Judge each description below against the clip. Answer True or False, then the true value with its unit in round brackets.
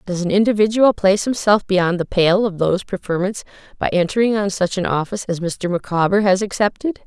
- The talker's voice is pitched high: True (195 Hz)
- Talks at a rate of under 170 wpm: False (185 wpm)